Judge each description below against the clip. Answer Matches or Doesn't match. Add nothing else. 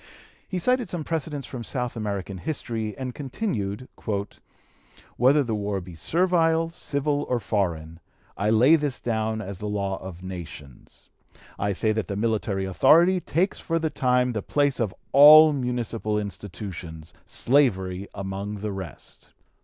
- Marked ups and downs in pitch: Matches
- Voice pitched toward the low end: Matches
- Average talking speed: Matches